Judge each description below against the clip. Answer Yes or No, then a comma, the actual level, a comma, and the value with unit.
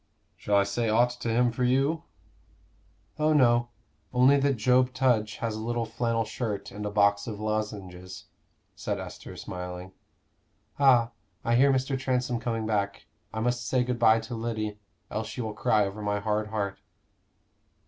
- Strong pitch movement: No, average, 2.8 semitones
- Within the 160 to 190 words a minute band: Yes, average, 165 wpm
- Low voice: Yes, low, 115 Hz